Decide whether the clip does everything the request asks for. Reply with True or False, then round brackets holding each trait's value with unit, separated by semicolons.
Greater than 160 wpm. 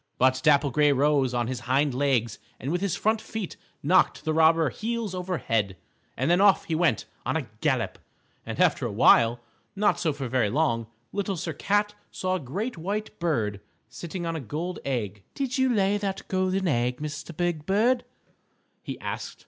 True (180 wpm)